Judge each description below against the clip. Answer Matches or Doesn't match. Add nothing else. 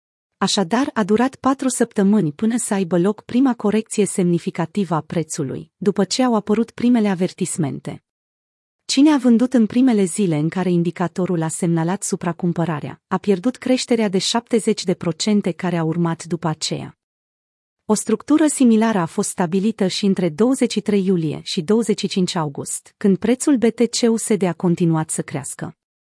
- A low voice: Doesn't match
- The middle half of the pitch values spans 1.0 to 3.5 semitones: Doesn't match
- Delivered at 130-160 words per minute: Matches